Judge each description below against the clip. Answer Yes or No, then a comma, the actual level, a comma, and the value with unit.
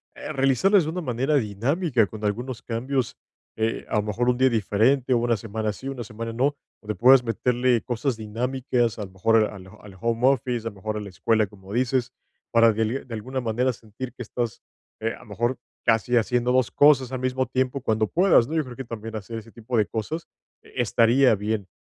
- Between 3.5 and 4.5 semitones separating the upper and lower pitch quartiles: No, average, 2.8 semitones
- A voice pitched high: No, low, 120 Hz